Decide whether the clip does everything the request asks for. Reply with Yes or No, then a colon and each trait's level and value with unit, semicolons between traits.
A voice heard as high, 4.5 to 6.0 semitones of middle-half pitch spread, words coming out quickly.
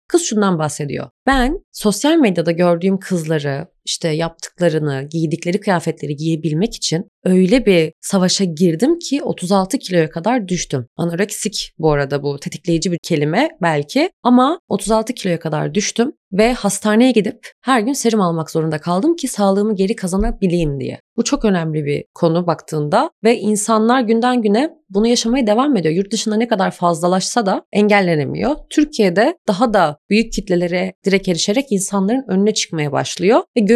Yes: high, 200 Hz; wide, 5.4 semitones; fast, 150 wpm